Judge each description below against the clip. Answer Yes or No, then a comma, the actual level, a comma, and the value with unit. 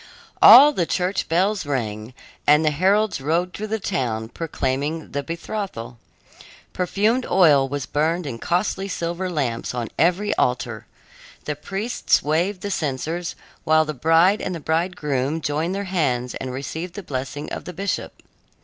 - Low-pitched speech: No, medium, 160 Hz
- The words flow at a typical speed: Yes, average, 150 wpm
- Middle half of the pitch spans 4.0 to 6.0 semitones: Yes, average, 5.3 semitones